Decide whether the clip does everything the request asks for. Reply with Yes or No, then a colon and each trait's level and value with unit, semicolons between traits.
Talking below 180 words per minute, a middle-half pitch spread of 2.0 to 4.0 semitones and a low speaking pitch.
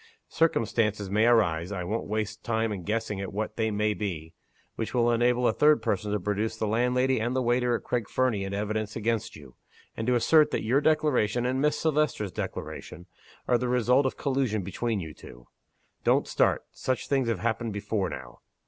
No: average, 195 wpm; average, 3.3 semitones; low, 110 Hz